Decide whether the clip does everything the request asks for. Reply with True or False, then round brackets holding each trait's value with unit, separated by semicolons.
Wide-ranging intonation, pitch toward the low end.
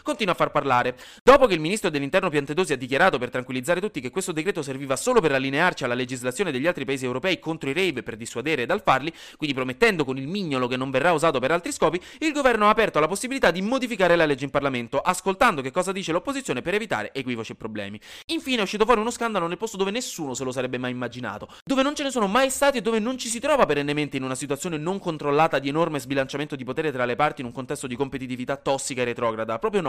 False (7.6 semitones; 155 Hz)